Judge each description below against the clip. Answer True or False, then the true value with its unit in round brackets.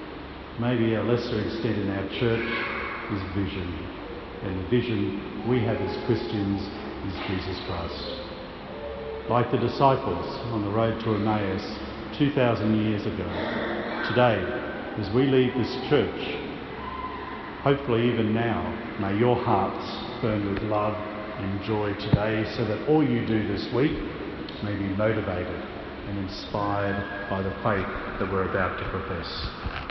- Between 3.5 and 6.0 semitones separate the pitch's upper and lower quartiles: False (2.8 semitones)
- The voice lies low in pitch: True (105 Hz)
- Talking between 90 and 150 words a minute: True (135 wpm)